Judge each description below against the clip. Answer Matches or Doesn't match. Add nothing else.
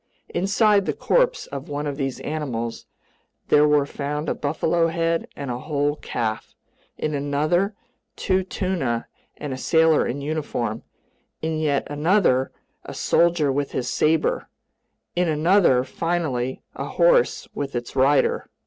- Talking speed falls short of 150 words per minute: Matches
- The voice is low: Doesn't match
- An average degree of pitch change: Matches